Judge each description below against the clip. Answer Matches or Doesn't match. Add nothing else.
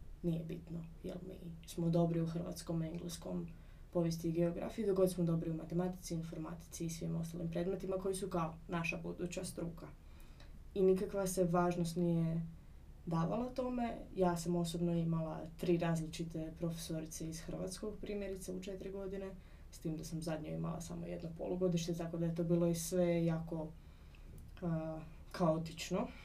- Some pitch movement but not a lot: Doesn't match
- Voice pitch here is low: Doesn't match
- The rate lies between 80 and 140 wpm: Doesn't match